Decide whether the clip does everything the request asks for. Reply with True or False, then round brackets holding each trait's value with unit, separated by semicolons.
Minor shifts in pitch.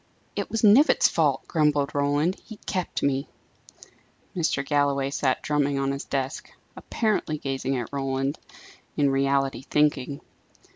True (1.7 semitones)